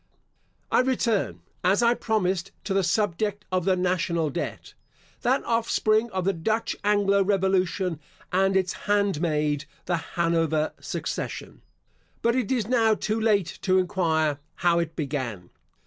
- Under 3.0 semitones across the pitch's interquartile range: No, average, 4.0 semitones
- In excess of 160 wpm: No, slow, 135 wpm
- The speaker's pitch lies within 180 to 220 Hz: Yes, high, 190 Hz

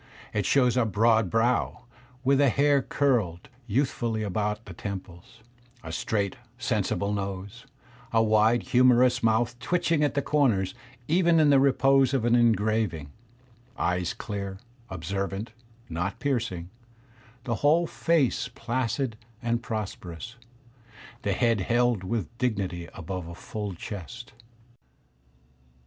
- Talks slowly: Yes, slow, 120 wpm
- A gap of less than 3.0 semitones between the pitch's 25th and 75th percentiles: No, average, 4.4 semitones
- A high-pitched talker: No, low, 115 Hz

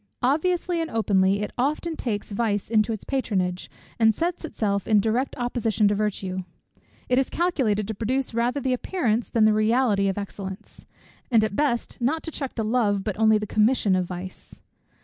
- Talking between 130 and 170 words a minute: No, average, 180 wpm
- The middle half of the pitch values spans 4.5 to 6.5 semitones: No, average, 4.0 semitones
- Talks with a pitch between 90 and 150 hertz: No, high, 220 Hz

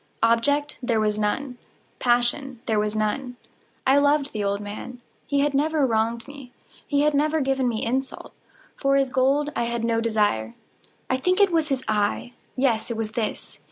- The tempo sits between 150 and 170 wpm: No, average, 180 wpm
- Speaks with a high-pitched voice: Yes, very high, 250 Hz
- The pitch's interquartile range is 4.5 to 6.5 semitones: No, average, 4.1 semitones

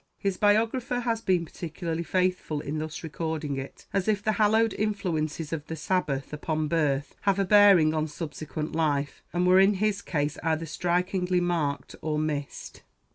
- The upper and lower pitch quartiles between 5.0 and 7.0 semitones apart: No, average, 4.3 semitones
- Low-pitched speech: No, medium, 165 Hz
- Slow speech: No, average, 165 wpm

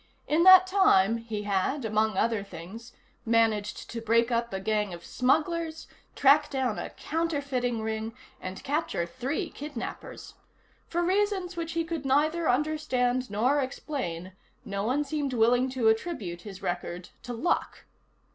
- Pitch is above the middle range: Yes, high, 245 Hz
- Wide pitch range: Yes, wide, 5.8 semitones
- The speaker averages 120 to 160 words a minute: Yes, average, 145 wpm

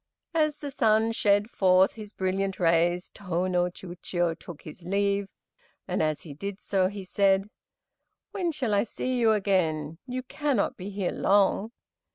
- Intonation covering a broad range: No, average, 3.2 semitones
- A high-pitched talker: Yes, high, 195 Hz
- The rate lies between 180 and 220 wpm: No, average, 160 wpm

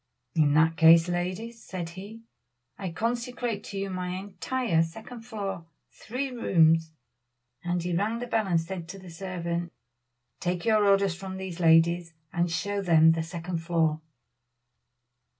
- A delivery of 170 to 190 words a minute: No, average, 150 wpm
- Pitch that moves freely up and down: No, average, 3.5 semitones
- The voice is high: No, medium, 180 Hz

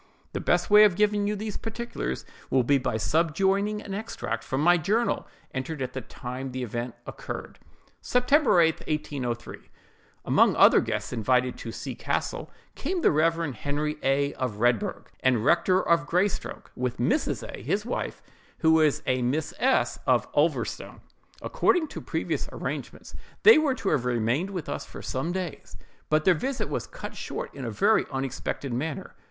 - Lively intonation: Yes, wide, 7.8 semitones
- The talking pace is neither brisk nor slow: Yes, average, 165 wpm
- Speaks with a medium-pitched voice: Yes, medium, 155 Hz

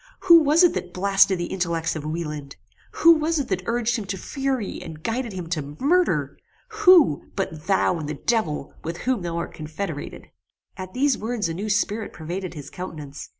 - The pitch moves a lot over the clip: Yes, wide, 7.0 semitones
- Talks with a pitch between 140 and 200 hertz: Yes, high, 190 Hz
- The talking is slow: No, average, 190 wpm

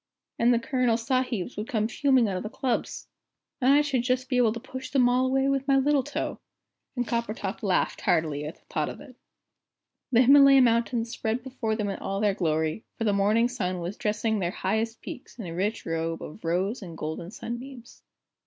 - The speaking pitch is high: Yes, high, 230 Hz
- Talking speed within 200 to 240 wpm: Yes, fast, 205 wpm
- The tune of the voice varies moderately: Yes, average, 4.5 semitones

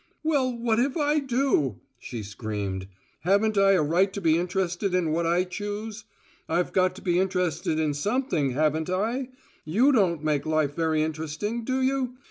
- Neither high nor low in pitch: Yes, medium, 180 Hz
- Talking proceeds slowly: No, average, 170 wpm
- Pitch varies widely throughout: Yes, wide, 6.2 semitones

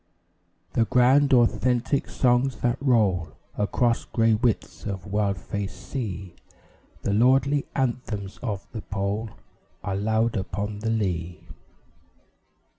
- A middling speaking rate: No, slow, 115 wpm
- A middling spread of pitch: Yes, average, 3.8 semitones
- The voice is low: Yes, low, 110 Hz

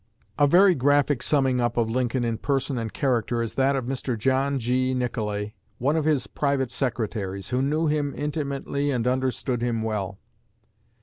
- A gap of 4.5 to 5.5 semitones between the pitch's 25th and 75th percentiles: No, average, 3.1 semitones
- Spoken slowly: No, average, 170 wpm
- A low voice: Yes, low, 130 Hz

